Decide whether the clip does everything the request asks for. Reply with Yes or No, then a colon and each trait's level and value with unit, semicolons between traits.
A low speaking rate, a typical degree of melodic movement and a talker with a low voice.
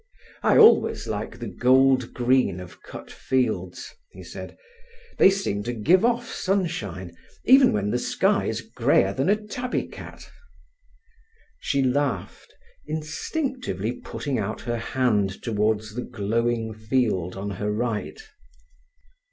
No: slow, 125 wpm; wide, 6.6 semitones; low, 120 Hz